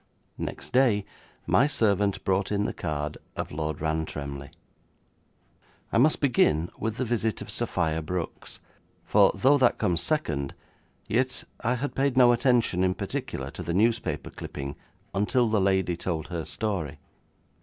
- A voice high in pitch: No, low, 100 Hz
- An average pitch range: No, wide, 7.1 semitones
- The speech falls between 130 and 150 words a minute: Yes, average, 145 wpm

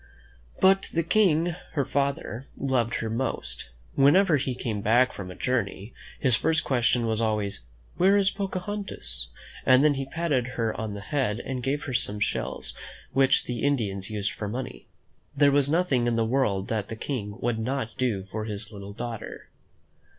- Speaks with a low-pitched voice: Yes, low, 125 Hz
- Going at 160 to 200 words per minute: Yes, average, 170 wpm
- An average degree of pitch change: Yes, average, 4.7 semitones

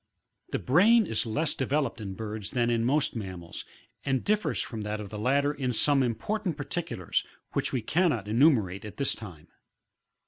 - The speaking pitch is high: No, low, 125 Hz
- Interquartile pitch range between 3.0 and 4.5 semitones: No, wide, 5.6 semitones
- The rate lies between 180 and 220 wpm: Yes, average, 185 wpm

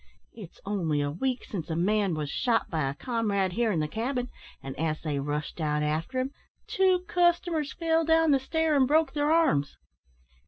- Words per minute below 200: Yes, average, 190 wpm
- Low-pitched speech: No, high, 220 Hz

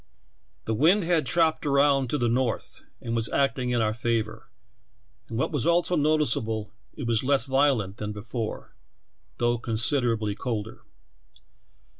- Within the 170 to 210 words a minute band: No, average, 140 wpm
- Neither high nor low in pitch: No, low, 120 Hz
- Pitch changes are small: No, average, 4.3 semitones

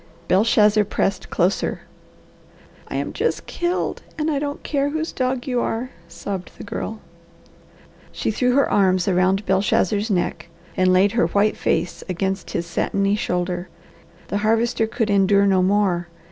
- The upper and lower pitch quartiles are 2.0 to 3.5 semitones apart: No, average, 3.9 semitones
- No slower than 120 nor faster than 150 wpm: Yes, average, 145 wpm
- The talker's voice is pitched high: Yes, high, 205 Hz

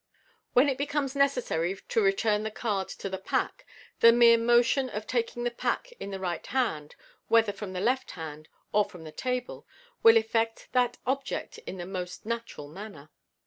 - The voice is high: Yes, high, 225 Hz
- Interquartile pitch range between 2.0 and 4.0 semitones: No, average, 4.8 semitones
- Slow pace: No, average, 180 wpm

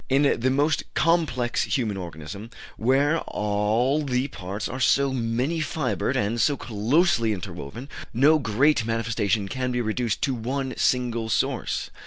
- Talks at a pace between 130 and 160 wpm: Yes, slow, 135 wpm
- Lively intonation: No, average, 4.1 semitones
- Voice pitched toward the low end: Yes, low, 125 Hz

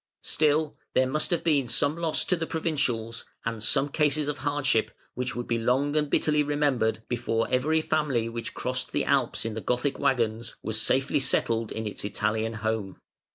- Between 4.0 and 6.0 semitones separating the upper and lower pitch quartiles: Yes, average, 4.6 semitones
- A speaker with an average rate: Yes, average, 180 wpm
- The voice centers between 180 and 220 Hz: No, low, 130 Hz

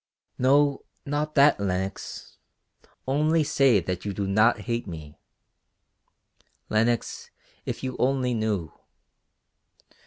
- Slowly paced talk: Yes, slow, 100 wpm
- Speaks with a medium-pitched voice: No, low, 120 Hz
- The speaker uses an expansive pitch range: Yes, wide, 5.9 semitones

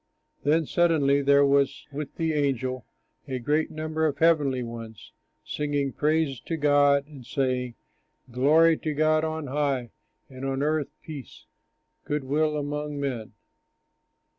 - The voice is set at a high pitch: No, medium, 145 Hz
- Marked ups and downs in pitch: No, narrow, 2.6 semitones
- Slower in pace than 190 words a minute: Yes, average, 140 wpm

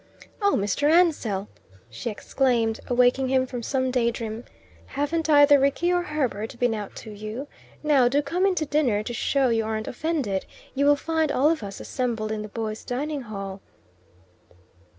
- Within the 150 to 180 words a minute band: Yes, average, 170 wpm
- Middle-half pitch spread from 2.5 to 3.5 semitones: No, average, 5.0 semitones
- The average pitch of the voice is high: Yes, very high, 250 Hz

